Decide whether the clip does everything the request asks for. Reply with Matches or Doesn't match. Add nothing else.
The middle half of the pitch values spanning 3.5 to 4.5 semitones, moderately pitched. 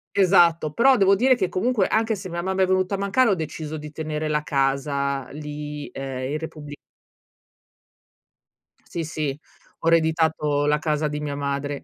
Matches